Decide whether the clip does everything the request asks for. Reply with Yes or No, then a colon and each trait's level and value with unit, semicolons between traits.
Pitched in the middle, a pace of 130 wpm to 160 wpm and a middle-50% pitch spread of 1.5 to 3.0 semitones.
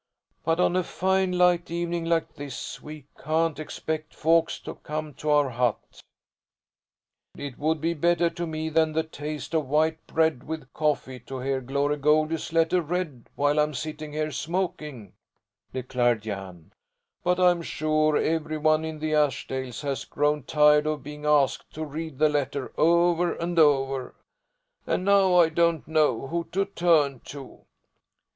Yes: medium, 155 Hz; average, 155 wpm; narrow, 2.5 semitones